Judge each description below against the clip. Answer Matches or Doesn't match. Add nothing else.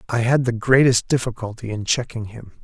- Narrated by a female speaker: Doesn't match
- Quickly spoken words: Doesn't match